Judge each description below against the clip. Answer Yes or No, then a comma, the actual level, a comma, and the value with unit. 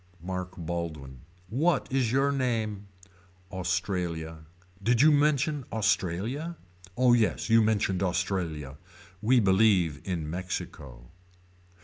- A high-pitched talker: No, very low, 95 Hz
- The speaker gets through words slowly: Yes, slow, 100 wpm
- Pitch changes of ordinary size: No, wide, 5.9 semitones